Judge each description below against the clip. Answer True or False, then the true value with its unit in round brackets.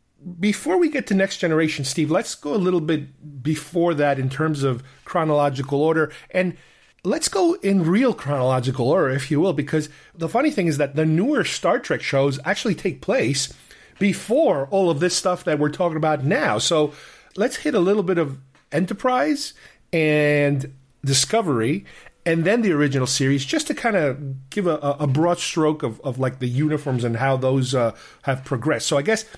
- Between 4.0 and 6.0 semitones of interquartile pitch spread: True (4.9 semitones)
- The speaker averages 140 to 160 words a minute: False (185 wpm)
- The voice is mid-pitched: True (155 Hz)